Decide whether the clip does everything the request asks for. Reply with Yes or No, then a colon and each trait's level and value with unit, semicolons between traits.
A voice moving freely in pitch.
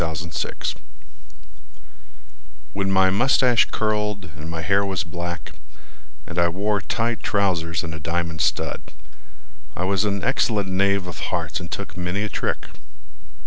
No: average, 3.3 semitones